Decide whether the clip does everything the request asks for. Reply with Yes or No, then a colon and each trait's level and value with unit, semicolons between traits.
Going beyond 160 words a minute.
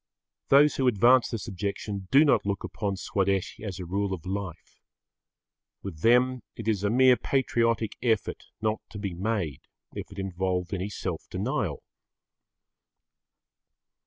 No: average, 140 wpm